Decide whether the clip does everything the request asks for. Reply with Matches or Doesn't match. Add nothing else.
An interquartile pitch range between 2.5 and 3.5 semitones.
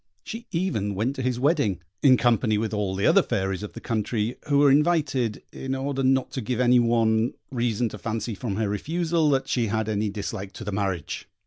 Doesn't match